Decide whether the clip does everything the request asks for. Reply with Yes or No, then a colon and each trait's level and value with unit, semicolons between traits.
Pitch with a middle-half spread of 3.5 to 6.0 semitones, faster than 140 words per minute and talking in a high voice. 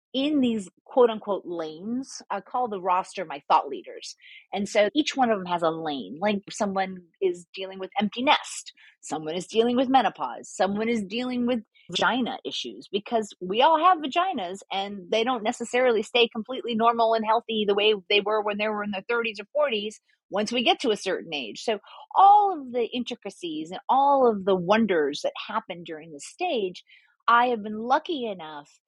Yes: average, 4.6 semitones; average, 190 wpm; high, 225 Hz